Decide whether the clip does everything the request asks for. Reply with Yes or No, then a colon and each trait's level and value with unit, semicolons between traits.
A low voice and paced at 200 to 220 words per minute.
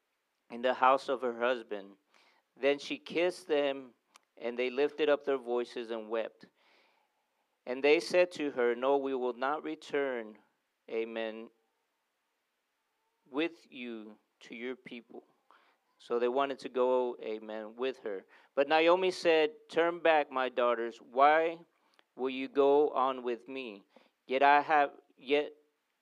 No: low, 130 Hz; average, 140 wpm